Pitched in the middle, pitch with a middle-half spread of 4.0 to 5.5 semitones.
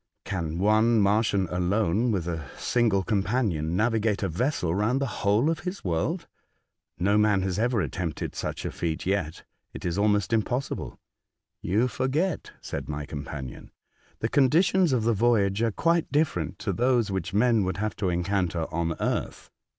No: low, 105 Hz; average, 5.1 semitones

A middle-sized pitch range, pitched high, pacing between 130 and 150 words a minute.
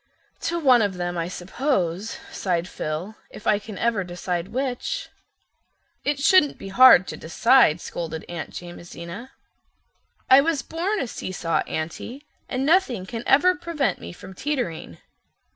No: wide, 7.8 semitones; high, 215 Hz; average, 145 wpm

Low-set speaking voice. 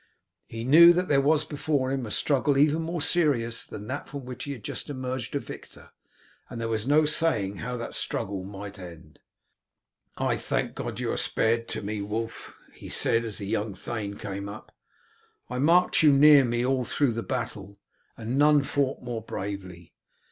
Yes: low, 120 Hz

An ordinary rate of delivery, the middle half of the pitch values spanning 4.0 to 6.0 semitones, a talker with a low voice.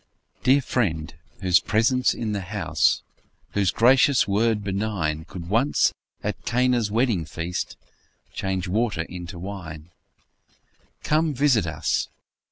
No: slow, 115 wpm; wide, 5.4 semitones; low, 100 Hz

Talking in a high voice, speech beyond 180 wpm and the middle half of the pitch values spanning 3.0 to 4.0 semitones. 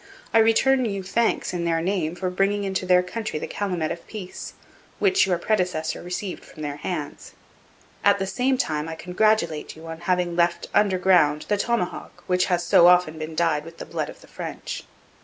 No: medium, 180 Hz; average, 195 wpm; average, 3.5 semitones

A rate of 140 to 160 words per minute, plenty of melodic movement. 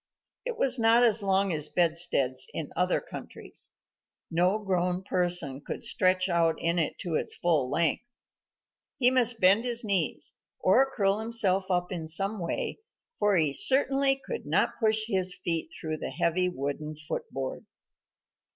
No: average, 155 wpm; average, 4.8 semitones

